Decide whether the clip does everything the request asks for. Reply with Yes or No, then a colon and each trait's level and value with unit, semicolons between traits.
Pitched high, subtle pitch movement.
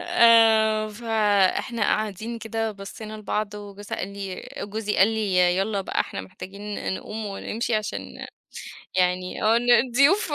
Yes: high, 215 Hz; narrow, 2.1 semitones